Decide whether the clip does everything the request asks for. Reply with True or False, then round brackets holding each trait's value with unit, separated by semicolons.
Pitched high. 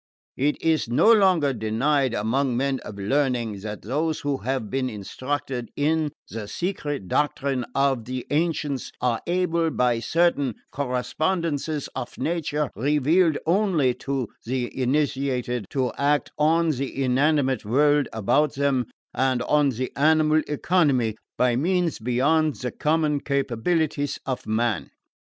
False (140 Hz)